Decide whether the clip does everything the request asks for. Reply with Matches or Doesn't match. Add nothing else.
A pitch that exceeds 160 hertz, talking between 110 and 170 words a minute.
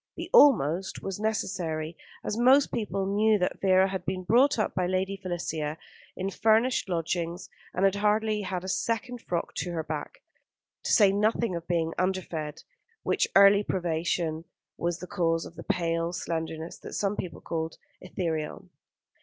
Matches